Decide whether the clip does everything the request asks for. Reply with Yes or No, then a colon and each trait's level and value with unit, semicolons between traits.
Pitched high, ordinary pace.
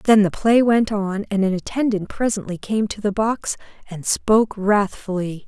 Yes: high, 205 Hz; average, 175 wpm